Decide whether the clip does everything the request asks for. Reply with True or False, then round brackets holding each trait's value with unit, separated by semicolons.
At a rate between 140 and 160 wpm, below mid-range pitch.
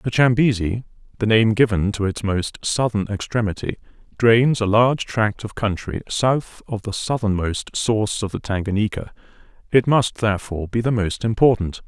True (155 wpm; 110 Hz)